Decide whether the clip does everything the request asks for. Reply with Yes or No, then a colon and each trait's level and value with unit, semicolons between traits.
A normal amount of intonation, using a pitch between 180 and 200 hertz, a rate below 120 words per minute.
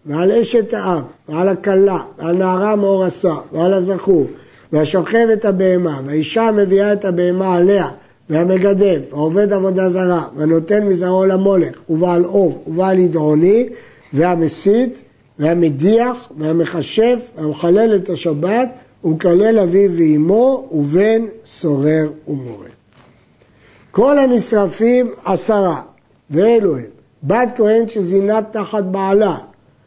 Yes: average, 4.5 semitones; medium, 185 Hz; slow, 100 wpm